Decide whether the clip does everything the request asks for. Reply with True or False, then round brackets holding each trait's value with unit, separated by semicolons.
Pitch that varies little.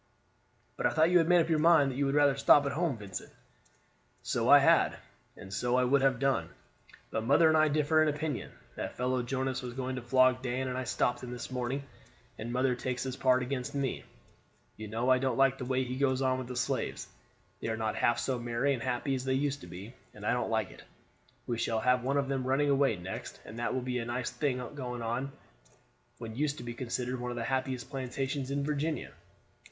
True (2.2 semitones)